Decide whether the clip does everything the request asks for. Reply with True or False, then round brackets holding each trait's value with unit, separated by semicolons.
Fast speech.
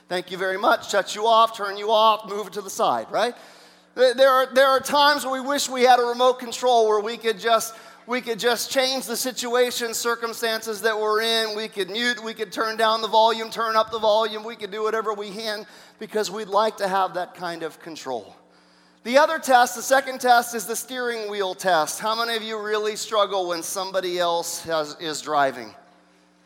True (215 wpm)